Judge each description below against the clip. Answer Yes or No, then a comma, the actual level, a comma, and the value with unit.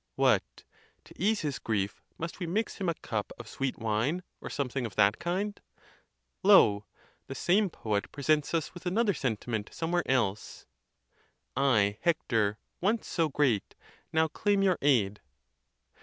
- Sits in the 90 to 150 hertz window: Yes, medium, 140 Hz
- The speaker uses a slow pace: No, average, 150 wpm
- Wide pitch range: Yes, wide, 8.3 semitones